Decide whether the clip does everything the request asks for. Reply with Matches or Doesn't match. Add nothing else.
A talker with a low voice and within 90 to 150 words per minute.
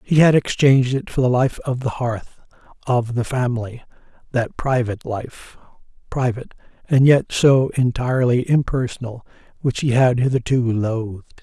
Matches